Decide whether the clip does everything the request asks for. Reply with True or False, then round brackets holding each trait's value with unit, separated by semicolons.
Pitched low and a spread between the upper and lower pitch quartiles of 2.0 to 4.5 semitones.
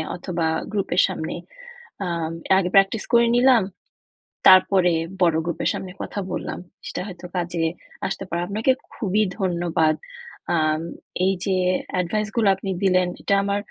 False (185 Hz; 2.8 semitones)